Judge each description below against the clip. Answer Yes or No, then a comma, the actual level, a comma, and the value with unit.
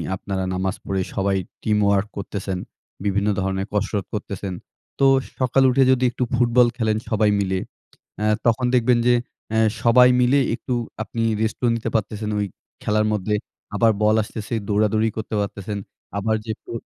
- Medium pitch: No, low, 110 Hz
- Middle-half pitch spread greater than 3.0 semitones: No, narrow, 2.6 semitones